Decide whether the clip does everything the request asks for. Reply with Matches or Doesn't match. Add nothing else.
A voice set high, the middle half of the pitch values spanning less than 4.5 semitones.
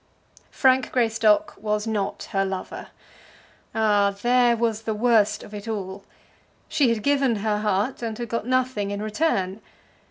Matches